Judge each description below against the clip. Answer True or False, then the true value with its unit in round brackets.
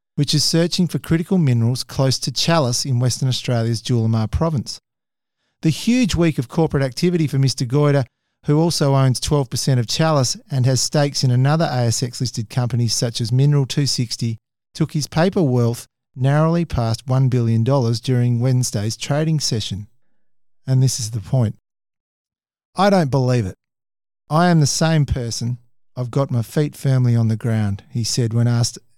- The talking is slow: False (165 wpm)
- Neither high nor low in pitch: False (130 Hz)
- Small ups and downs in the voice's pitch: False (3.9 semitones)